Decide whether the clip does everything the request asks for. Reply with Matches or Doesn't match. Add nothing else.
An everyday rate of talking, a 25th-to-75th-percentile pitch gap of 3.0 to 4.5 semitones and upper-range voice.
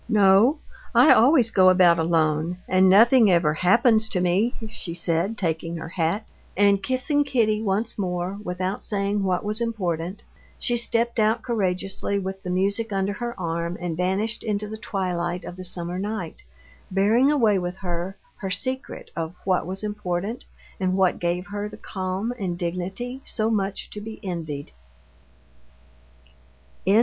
Matches